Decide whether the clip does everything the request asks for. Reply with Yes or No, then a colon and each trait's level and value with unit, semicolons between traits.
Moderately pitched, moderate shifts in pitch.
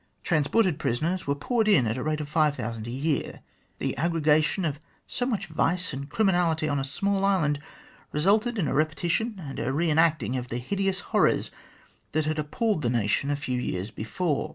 Yes: medium, 155 Hz; average, 4.8 semitones